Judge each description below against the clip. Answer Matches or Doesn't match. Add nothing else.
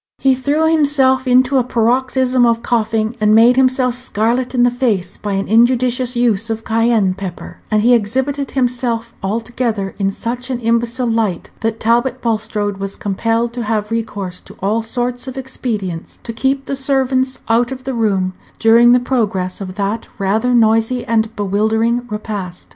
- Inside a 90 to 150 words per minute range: Doesn't match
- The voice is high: Matches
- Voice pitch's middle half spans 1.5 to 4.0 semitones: Matches